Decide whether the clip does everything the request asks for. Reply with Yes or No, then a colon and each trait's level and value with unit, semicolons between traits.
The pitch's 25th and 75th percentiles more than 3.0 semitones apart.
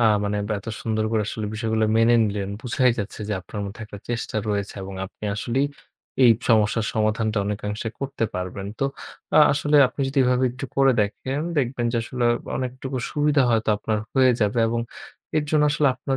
Yes: average, 3.7 semitones